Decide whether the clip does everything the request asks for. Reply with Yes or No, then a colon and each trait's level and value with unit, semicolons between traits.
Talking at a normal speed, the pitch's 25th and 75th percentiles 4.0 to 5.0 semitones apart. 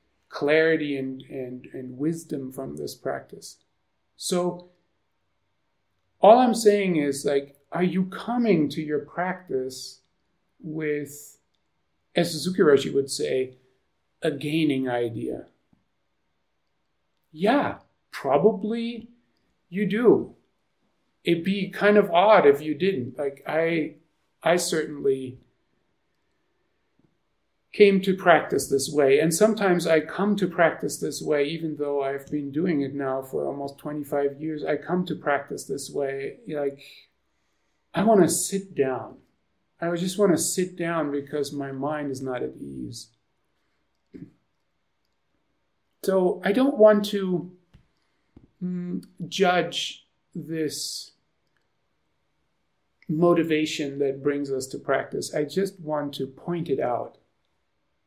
No: slow, 120 wpm; average, 4.5 semitones